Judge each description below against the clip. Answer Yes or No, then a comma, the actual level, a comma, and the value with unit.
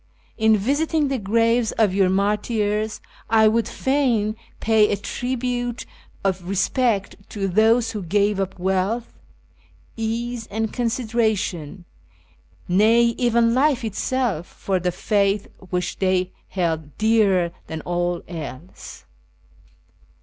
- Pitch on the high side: Yes, high, 215 Hz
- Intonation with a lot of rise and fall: No, average, 3.6 semitones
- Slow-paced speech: Yes, slow, 115 wpm